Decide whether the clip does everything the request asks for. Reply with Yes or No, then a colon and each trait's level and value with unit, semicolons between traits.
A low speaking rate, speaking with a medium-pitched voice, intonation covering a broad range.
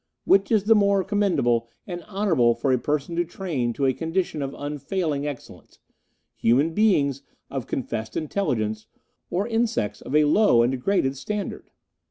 No: average, 160 wpm; medium, 150 Hz; wide, 7.3 semitones